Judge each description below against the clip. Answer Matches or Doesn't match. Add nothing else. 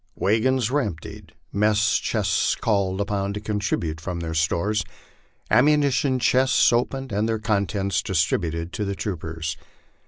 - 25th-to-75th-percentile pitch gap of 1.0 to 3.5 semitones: Doesn't match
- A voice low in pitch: Matches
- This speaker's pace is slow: Matches